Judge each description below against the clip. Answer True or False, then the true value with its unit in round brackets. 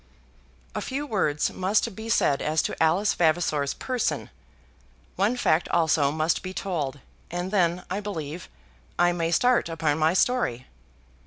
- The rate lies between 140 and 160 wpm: True (145 wpm)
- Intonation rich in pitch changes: False (4.4 semitones)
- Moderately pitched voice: True (175 Hz)